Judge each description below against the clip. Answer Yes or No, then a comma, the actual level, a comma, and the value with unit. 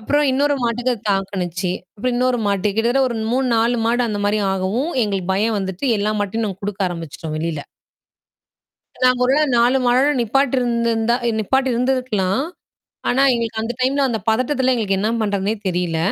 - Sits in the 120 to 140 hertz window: No, high, 225 Hz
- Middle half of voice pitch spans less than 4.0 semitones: No, average, 4.3 semitones